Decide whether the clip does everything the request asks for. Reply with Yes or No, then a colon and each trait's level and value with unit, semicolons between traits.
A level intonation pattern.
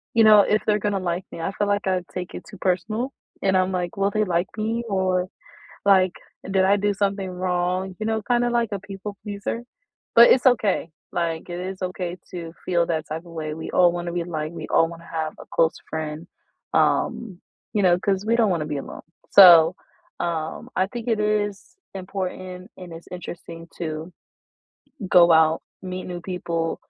No: average, 3.1 semitones